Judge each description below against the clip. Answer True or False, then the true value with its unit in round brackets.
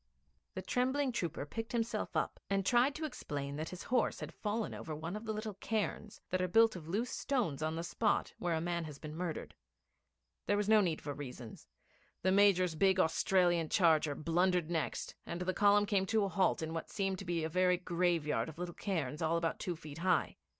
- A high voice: False (180 Hz)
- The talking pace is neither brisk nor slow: False (210 wpm)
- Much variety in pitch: False (4.1 semitones)